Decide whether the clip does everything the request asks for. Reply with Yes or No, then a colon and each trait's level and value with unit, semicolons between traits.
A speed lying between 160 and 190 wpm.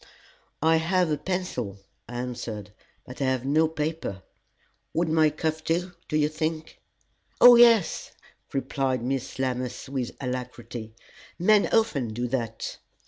No: slow, 135 wpm